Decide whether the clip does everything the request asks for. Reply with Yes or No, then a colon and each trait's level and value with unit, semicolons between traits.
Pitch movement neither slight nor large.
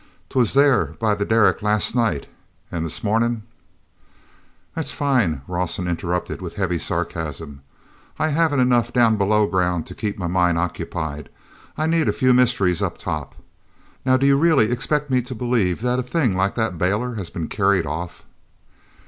No: wide, 6.1 semitones